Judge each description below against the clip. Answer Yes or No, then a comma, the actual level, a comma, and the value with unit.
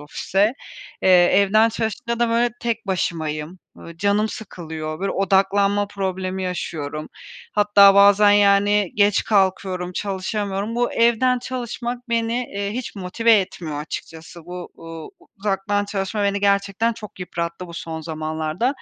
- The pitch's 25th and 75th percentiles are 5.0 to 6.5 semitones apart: No, average, 3.0 semitones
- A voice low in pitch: No, high, 200 Hz